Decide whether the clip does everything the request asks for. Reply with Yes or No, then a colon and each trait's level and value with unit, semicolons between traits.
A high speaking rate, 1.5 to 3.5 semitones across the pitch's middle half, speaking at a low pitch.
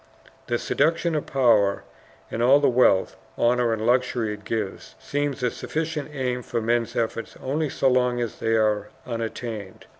No: average, 160 wpm; average, 3.0 semitones; low, 120 Hz